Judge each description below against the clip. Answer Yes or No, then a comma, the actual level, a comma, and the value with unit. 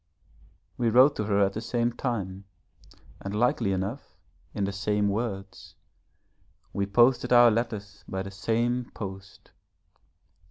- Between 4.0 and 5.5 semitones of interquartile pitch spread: No, average, 3.4 semitones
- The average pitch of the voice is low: Yes, low, 105 Hz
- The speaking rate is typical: No, slow, 130 wpm